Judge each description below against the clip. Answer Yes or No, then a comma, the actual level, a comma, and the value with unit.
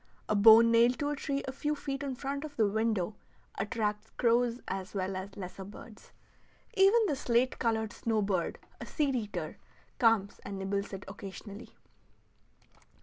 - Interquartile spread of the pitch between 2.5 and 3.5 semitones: No, average, 4.6 semitones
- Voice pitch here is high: Yes, high, 225 Hz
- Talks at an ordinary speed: Yes, average, 160 wpm